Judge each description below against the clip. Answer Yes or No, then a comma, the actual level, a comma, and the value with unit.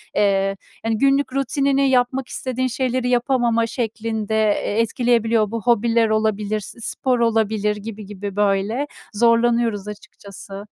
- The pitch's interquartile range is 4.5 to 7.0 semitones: No, average, 2.8 semitones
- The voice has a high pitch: Yes, high, 225 Hz